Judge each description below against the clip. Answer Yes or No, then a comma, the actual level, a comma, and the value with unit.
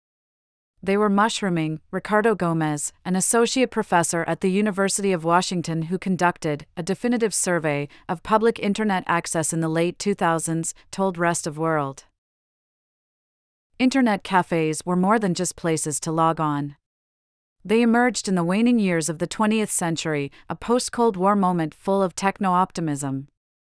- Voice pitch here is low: No, medium, 180 Hz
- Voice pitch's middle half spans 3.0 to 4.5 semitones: Yes, average, 3.9 semitones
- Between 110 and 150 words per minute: Yes, average, 145 wpm